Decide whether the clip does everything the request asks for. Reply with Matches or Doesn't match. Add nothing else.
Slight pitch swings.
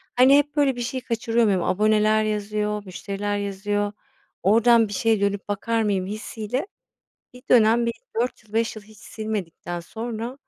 Matches